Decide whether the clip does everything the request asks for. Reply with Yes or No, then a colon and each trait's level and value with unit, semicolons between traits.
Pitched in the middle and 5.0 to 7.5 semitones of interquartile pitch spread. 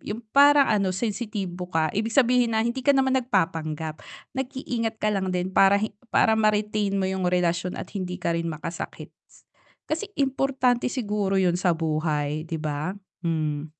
No: high, 195 Hz; wide, 5.6 semitones